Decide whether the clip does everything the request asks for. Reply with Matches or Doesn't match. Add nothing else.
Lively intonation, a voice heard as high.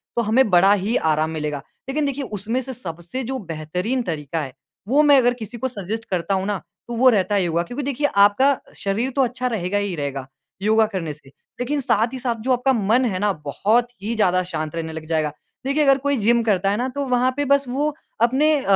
Matches